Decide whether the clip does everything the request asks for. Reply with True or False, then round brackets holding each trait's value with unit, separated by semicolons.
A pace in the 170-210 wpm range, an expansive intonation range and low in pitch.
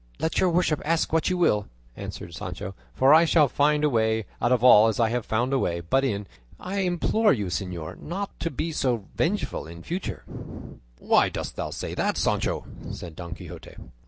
True (200 wpm; 7.9 semitones; 130 Hz)